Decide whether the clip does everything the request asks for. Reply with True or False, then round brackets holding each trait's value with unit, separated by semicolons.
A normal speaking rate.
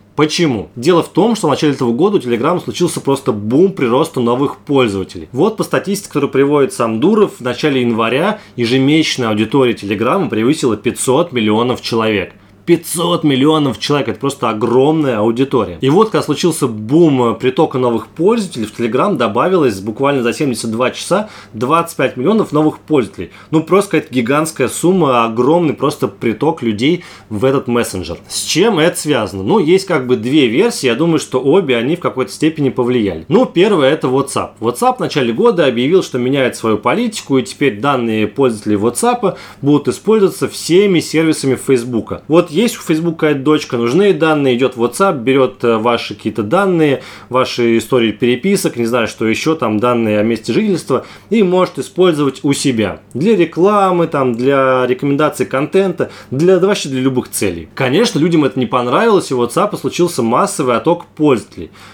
False (165 wpm)